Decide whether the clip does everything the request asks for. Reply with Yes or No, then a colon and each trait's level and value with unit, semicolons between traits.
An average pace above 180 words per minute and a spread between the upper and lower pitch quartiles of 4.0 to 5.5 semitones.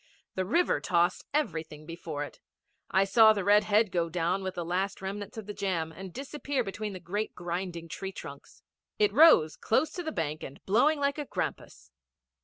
Yes: average, 190 wpm; average, 4.3 semitones